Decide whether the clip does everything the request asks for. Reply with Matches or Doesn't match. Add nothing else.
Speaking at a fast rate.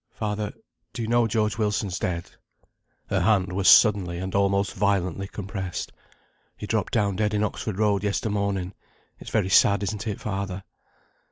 Doesn't match